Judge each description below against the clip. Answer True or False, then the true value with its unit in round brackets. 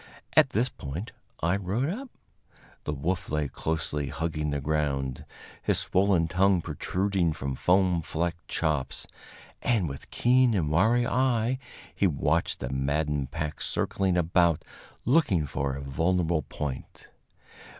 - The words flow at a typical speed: False (130 wpm)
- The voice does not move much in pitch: False (4.8 semitones)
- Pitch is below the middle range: True (85 Hz)